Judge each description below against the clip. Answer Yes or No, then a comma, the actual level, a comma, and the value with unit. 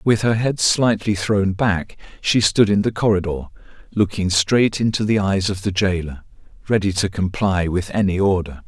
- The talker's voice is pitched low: Yes, low, 100 Hz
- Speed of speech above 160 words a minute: Yes, average, 175 wpm